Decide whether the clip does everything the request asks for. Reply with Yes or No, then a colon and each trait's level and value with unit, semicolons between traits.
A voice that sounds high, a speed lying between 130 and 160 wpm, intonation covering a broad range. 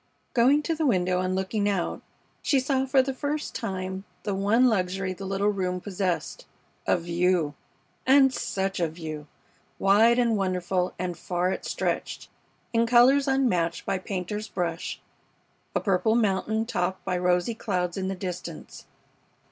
No: high, 195 Hz; average, 150 wpm; average, 4.4 semitones